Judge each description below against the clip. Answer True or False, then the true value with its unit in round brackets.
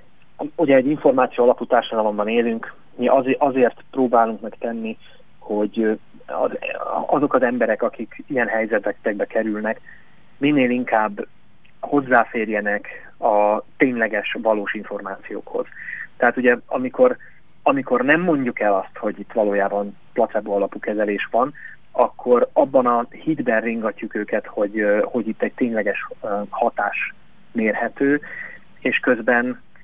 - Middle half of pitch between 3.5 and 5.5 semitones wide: True (3.8 semitones)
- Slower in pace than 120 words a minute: True (110 wpm)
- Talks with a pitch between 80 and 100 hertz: False (115 Hz)